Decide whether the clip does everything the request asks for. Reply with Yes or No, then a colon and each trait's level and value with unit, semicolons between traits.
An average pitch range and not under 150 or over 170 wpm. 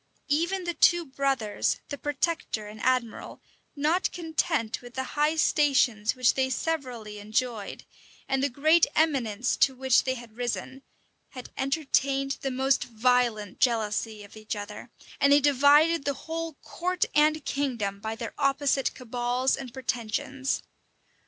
No: average, 3.8 semitones; average, 140 wpm